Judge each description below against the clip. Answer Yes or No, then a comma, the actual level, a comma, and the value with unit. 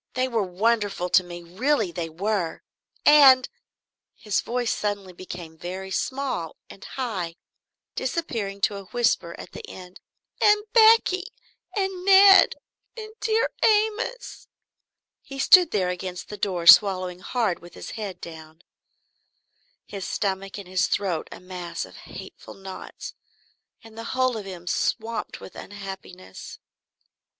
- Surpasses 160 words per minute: No, slow, 135 wpm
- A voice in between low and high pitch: No, high, 200 Hz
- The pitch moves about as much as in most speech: No, wide, 6.2 semitones